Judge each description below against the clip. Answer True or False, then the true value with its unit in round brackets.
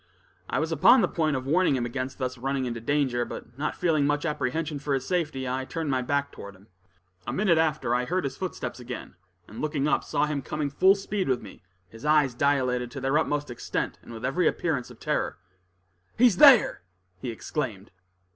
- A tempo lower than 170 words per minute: False (205 wpm)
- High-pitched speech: False (140 Hz)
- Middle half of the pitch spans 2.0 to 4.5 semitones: True (3.7 semitones)